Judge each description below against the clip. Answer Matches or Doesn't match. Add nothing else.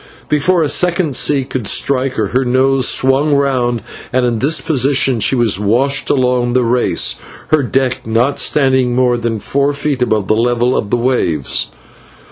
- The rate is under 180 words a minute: Matches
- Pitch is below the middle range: Matches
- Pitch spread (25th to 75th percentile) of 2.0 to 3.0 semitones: Matches